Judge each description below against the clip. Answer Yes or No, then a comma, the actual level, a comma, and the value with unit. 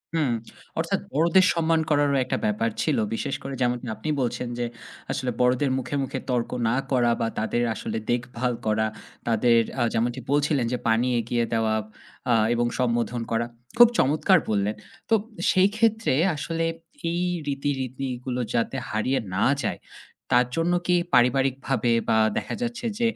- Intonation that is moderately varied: Yes, average, 3.7 semitones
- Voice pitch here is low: Yes, low, 125 Hz